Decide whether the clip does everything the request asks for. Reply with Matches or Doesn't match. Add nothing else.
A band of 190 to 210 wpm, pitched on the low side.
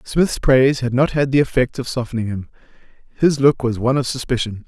Matches